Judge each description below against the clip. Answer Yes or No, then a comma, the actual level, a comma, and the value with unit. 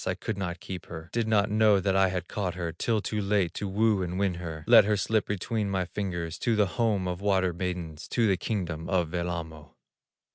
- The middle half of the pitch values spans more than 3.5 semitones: No, average, 3.0 semitones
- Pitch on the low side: Yes, very low, 95 Hz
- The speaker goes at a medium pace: No, fast, 220 wpm